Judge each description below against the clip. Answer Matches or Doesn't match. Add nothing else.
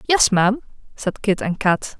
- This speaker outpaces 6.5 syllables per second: Doesn't match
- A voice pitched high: Matches